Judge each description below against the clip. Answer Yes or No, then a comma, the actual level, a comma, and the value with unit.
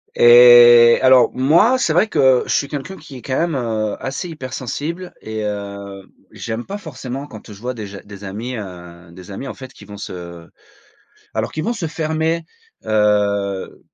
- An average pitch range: No, wide, 6.2 semitones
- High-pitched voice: No, low, 120 Hz